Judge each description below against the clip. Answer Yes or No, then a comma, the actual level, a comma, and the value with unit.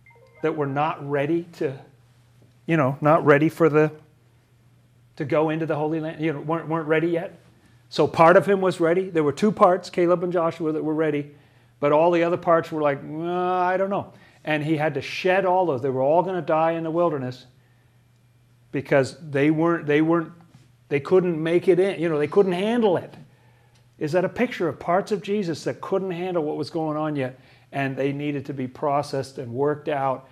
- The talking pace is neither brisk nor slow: No, fast, 210 wpm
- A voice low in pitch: No, medium, 155 Hz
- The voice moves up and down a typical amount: Yes, average, 3.9 semitones